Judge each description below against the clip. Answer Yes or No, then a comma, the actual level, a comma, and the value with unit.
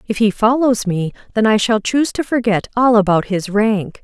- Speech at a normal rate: No, fast, 210 wpm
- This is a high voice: Yes, high, 220 Hz